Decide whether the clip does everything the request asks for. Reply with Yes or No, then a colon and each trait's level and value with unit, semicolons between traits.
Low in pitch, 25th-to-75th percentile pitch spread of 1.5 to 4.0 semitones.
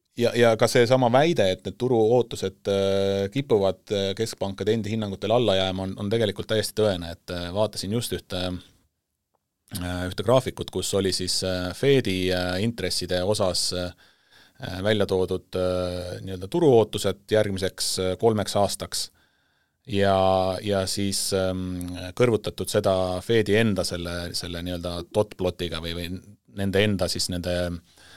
Yes: very low, 95 Hz; average, 2.8 semitones